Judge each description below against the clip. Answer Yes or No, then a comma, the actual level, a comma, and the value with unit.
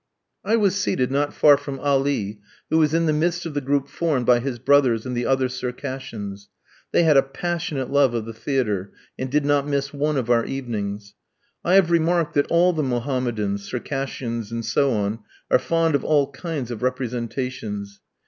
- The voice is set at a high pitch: No, low, 135 Hz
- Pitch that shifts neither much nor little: Yes, average, 3.9 semitones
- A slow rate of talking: No, average, 185 wpm